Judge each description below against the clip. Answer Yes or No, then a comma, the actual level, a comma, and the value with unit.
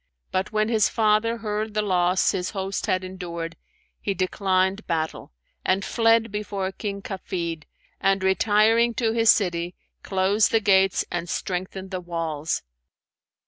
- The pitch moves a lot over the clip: No, average, 2.8 semitones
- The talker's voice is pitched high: Yes, high, 195 Hz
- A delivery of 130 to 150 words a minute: Yes, average, 140 wpm